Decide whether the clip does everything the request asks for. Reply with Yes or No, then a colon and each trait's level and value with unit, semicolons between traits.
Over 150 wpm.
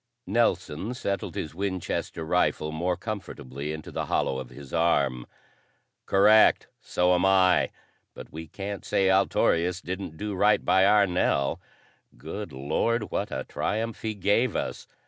No: average, 145 wpm